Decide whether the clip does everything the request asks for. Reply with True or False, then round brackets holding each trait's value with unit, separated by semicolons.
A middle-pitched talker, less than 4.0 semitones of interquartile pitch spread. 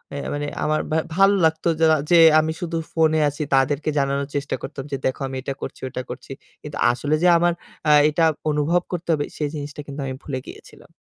True (150 Hz; 2.4 semitones)